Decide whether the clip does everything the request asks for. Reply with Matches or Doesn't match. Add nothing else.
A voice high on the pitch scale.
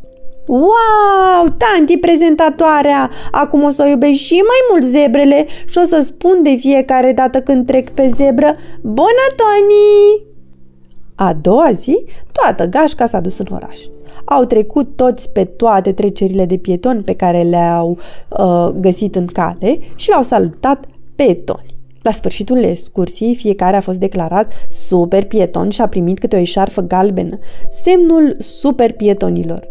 Matches